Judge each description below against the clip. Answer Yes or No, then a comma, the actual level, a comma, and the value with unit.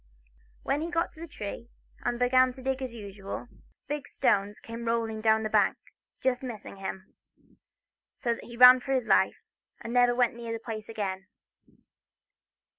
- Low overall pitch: No, high, 235 Hz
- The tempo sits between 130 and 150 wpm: No, average, 170 wpm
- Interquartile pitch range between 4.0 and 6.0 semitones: No, average, 2.8 semitones